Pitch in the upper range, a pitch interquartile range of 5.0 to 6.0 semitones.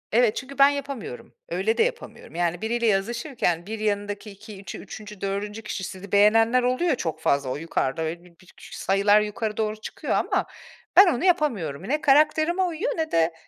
Yes: high, 215 Hz; wide, 5.6 semitones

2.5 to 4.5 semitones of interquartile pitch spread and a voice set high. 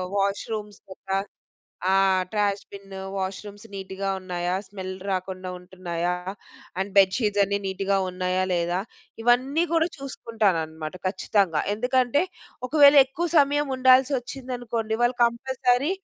No: average, 4.9 semitones; high, 200 Hz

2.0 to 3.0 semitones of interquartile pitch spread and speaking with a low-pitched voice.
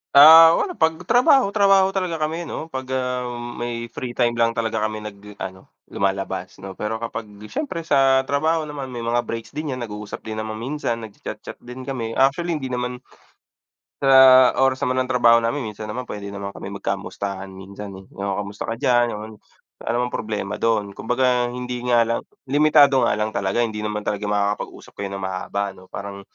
No: average, 4.3 semitones; low, 120 Hz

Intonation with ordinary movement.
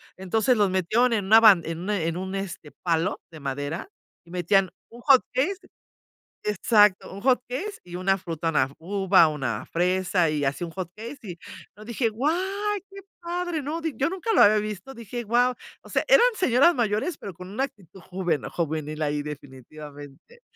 No: wide, 6.7 semitones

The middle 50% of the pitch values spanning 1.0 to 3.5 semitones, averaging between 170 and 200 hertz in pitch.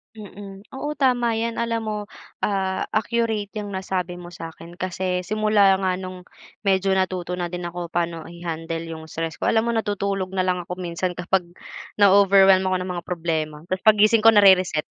Yes: average, 2.8 semitones; high, 190 Hz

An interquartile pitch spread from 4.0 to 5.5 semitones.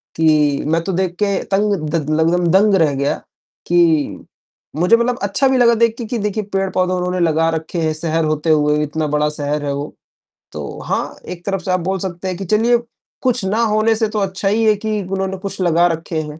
Yes: average, 4.6 semitones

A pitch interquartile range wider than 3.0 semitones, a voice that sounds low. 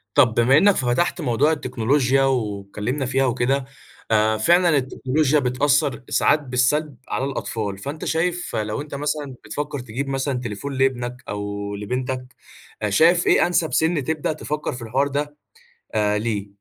Yes: average, 3.9 semitones; low, 130 Hz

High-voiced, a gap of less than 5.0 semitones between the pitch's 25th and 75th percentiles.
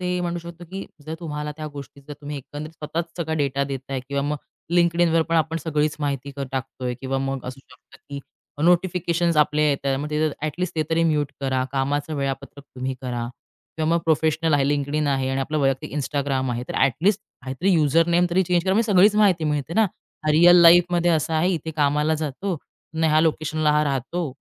No: medium, 150 Hz; average, 3.3 semitones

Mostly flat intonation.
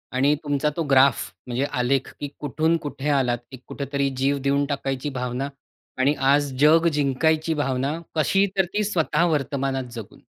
Yes: narrow, 2.2 semitones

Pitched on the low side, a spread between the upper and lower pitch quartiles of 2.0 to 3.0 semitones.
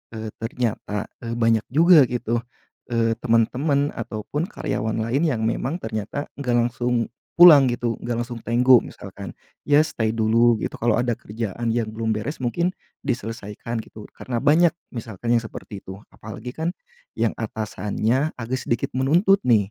Yes: low, 120 Hz; average, 2.7 semitones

